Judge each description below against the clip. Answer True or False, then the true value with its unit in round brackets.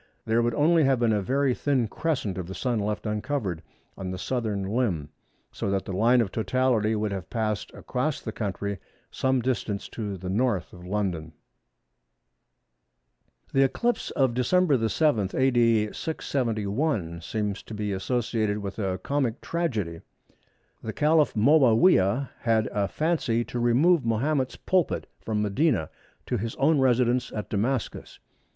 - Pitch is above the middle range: False (115 Hz)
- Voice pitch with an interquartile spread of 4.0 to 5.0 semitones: True (4.6 semitones)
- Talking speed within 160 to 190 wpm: False (145 wpm)